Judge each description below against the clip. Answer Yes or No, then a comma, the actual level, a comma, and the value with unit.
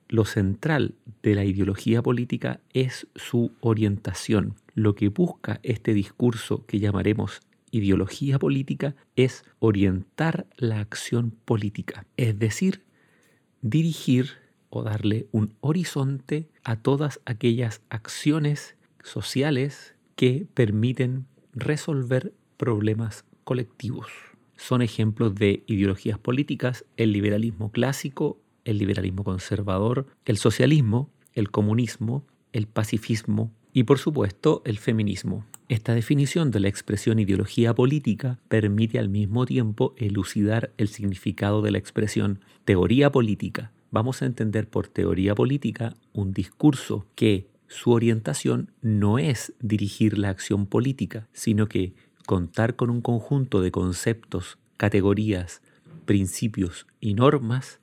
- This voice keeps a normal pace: No, slow, 115 wpm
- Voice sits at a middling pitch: No, low, 115 Hz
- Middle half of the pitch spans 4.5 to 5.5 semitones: No, average, 3.7 semitones